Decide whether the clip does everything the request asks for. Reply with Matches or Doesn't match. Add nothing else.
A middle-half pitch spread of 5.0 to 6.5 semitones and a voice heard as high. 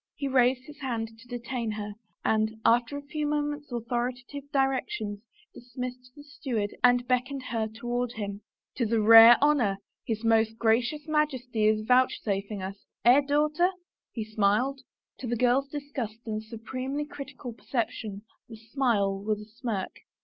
Doesn't match